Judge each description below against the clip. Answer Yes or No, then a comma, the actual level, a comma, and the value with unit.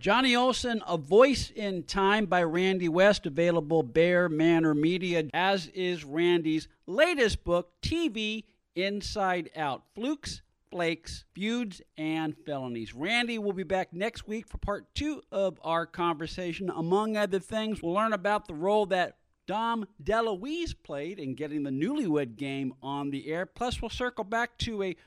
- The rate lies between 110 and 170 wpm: Yes, average, 155 wpm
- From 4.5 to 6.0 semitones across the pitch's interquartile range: Yes, average, 4.8 semitones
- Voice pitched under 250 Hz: Yes, medium, 185 Hz